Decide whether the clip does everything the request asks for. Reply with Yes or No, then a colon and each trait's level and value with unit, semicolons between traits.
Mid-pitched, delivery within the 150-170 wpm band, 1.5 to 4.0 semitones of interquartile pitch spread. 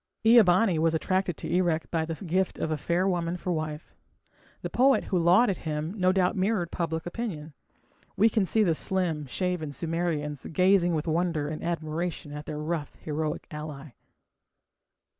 Yes: medium, 170 Hz; average, 165 wpm; average, 2.9 semitones